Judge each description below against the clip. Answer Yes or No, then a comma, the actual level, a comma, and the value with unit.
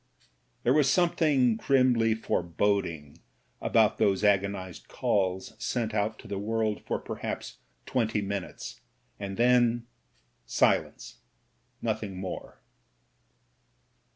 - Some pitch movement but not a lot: Yes, average, 3.6 semitones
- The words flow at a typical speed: No, slow, 100 wpm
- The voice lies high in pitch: No, low, 105 Hz